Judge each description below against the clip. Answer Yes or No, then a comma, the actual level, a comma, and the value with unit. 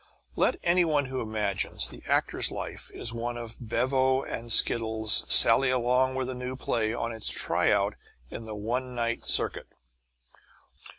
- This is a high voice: No, low, 120 Hz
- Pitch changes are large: No, narrow, 2.4 semitones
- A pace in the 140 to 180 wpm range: Yes, average, 160 wpm